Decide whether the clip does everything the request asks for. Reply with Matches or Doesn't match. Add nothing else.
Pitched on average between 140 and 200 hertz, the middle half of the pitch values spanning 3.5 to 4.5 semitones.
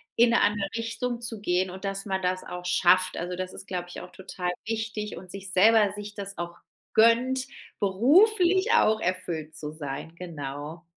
Matches